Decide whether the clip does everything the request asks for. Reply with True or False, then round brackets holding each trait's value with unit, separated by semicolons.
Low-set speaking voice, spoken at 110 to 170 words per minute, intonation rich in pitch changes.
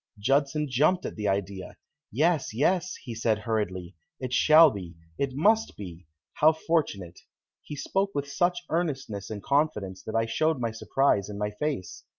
True (130 Hz; 160 wpm; 7.1 semitones)